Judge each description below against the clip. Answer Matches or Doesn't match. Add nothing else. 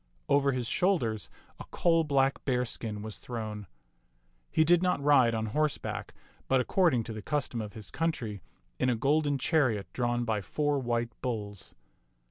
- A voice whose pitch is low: Matches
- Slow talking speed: Doesn't match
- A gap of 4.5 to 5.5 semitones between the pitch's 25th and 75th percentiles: Matches